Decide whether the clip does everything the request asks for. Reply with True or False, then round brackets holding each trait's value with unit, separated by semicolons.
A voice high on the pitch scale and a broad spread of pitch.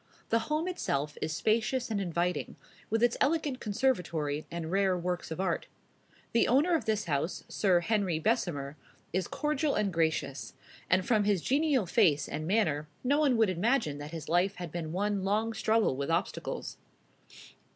True (195 Hz; 5.7 semitones)